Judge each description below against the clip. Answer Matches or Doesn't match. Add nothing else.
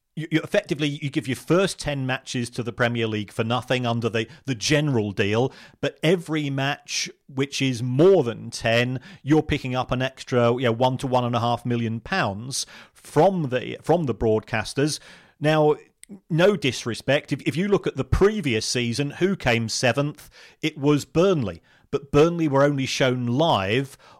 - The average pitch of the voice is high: Doesn't match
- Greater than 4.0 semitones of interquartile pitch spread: Matches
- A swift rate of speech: Doesn't match